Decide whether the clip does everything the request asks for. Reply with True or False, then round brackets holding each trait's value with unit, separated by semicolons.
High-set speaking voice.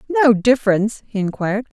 True (225 Hz)